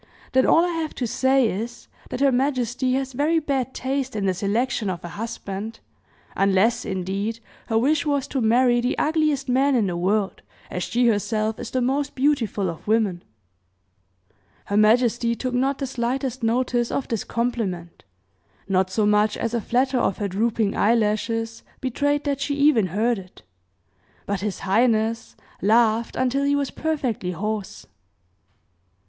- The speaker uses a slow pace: No, average, 160 wpm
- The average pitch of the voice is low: No, high, 235 Hz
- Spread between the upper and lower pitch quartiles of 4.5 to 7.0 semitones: No, average, 4.0 semitones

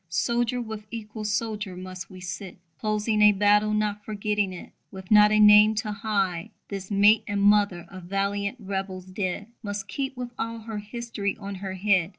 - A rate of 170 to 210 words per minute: Yes, average, 175 wpm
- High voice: Yes, high, 205 Hz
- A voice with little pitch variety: Yes, narrow, 1.7 semitones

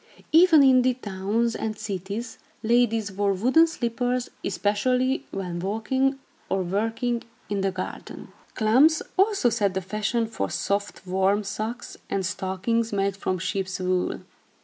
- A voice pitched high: Yes, high, 215 Hz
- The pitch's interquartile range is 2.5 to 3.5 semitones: No, average, 4.1 semitones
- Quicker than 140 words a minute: No, slow, 135 wpm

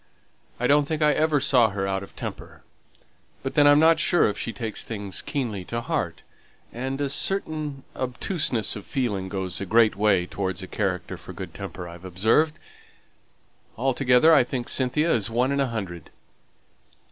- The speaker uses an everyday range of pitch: No, wide, 6.3 semitones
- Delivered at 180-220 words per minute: No, average, 170 wpm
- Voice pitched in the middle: No, low, 120 Hz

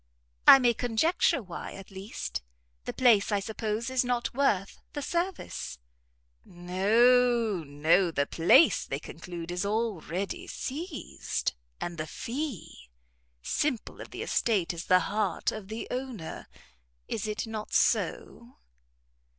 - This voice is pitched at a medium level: No, high, 215 Hz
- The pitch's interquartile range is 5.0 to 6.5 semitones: Yes, wide, 5.4 semitones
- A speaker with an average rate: No, slow, 125 wpm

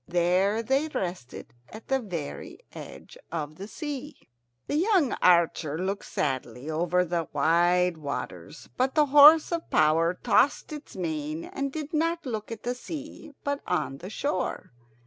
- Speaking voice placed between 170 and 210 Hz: Yes, high, 190 Hz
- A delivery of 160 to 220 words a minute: No, average, 150 wpm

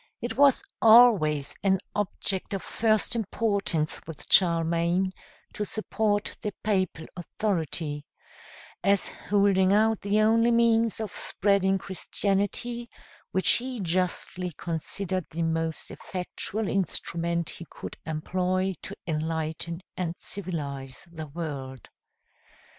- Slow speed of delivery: Yes, slow, 110 wpm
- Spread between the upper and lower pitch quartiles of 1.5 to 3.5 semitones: No, average, 4.1 semitones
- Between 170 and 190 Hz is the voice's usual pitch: Yes, medium, 185 Hz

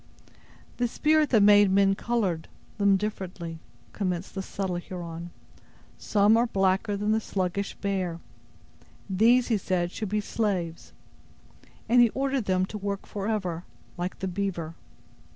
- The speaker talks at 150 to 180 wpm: No, slow, 135 wpm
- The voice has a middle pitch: No, high, 195 Hz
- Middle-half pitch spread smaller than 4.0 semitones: Yes, average, 2.7 semitones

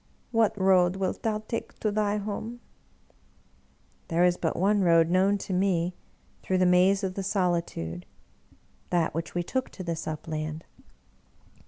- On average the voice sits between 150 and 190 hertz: Yes, medium, 185 Hz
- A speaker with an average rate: Yes, average, 165 wpm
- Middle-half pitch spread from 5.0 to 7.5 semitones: No, average, 3.1 semitones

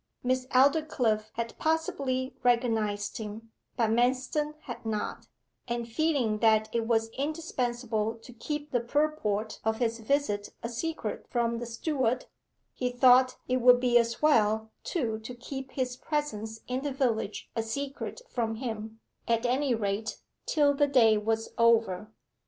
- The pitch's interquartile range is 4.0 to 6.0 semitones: No, average, 3.0 semitones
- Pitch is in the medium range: No, high, 240 Hz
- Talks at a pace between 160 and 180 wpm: No, average, 145 wpm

